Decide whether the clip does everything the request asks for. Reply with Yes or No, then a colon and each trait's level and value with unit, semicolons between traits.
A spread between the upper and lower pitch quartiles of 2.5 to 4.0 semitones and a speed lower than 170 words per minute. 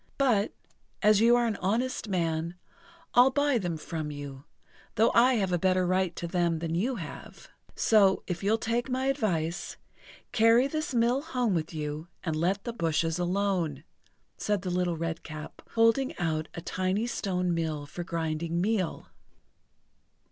No: wide, 5.6 semitones; average, 155 wpm